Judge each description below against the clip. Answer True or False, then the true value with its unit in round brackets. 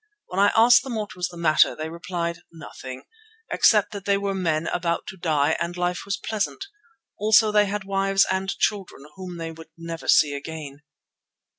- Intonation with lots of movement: False (3.5 semitones)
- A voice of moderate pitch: True (180 Hz)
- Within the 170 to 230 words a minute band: True (180 wpm)